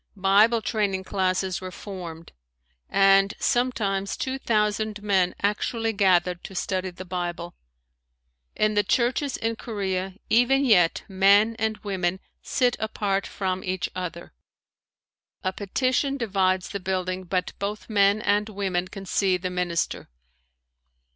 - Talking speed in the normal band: No, slow, 130 wpm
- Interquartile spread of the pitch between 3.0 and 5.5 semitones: No, narrow, 2.5 semitones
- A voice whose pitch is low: No, high, 195 Hz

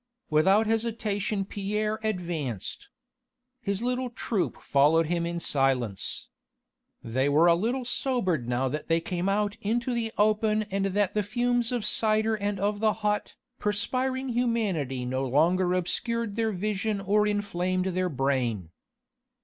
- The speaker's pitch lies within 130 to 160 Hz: No, high, 200 Hz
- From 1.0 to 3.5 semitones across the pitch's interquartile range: No, average, 4.7 semitones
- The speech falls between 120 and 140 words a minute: Yes, slow, 135 wpm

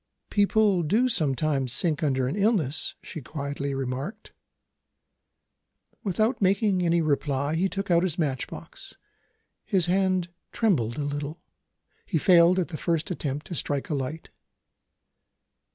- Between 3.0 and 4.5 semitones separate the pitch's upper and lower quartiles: No, average, 5.0 semitones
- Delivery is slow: Yes, slow, 130 wpm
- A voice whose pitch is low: No, medium, 165 Hz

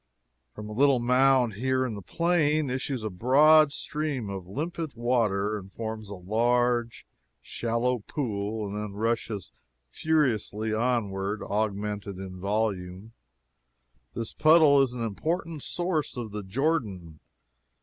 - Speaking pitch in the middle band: No, low, 115 Hz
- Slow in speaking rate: Yes, slow, 130 wpm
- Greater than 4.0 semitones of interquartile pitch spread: Yes, average, 4.8 semitones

